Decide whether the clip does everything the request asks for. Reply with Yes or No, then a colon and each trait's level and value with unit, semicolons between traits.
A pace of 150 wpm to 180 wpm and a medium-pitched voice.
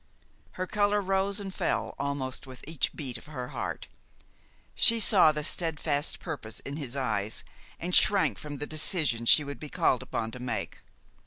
Yes: average, 170 wpm; medium, 150 Hz